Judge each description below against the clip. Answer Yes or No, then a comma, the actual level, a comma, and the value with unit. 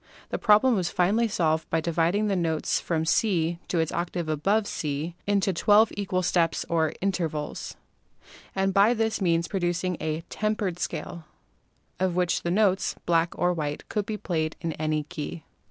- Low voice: No, medium, 175 Hz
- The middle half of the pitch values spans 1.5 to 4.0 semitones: Yes, average, 3.5 semitones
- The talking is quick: No, average, 170 wpm